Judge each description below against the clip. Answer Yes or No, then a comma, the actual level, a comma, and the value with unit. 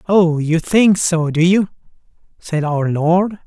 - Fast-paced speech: No, average, 155 wpm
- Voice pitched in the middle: Yes, medium, 170 Hz